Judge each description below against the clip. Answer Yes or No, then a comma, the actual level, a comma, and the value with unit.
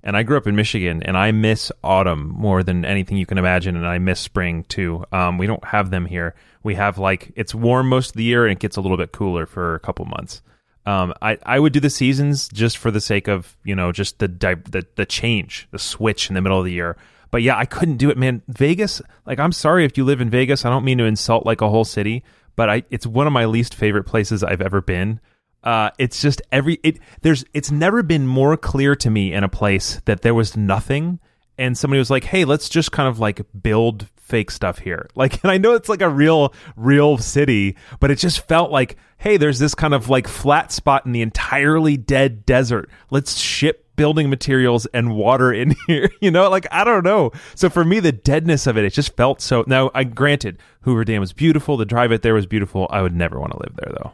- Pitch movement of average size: No, wide, 5.9 semitones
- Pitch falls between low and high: No, low, 115 Hz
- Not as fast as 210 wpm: No, fast, 245 wpm